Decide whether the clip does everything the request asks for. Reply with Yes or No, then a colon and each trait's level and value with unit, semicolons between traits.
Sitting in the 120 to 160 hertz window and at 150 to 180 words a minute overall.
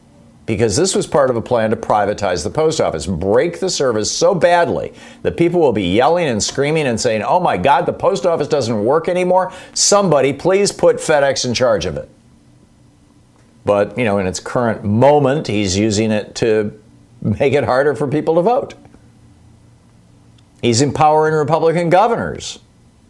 Yes: medium, 140 Hz; average, 170 wpm